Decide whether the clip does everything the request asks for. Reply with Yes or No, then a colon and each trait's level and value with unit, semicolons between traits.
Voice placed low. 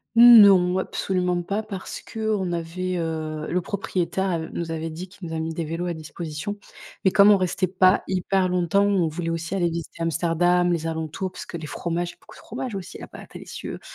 No: medium, 175 Hz